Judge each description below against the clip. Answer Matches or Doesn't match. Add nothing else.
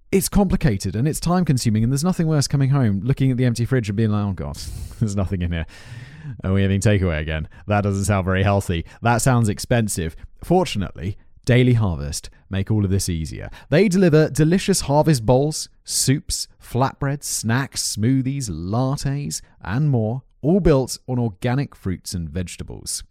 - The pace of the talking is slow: Doesn't match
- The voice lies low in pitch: Matches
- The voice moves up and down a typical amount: Doesn't match